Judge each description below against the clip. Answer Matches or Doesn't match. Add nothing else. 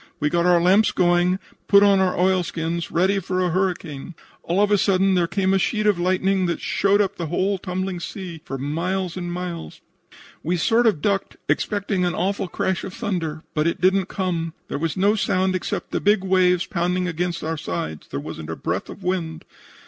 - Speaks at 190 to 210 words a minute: Matches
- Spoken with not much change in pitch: Matches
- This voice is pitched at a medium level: Matches